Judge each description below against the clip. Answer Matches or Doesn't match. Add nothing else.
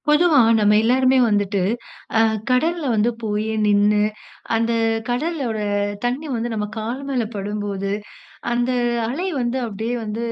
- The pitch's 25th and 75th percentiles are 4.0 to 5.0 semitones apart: Doesn't match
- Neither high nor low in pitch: Doesn't match